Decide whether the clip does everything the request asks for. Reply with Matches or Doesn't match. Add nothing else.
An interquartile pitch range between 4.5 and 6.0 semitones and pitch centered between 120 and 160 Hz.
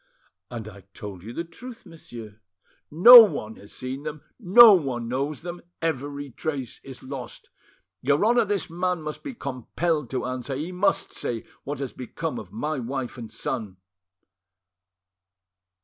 Matches